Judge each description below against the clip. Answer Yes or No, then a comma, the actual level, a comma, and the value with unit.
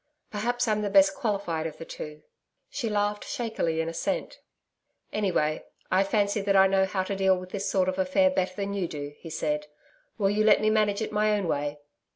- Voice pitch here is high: Yes, high, 195 Hz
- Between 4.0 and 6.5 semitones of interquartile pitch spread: No, average, 3.3 semitones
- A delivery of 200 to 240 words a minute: Yes, fast, 205 wpm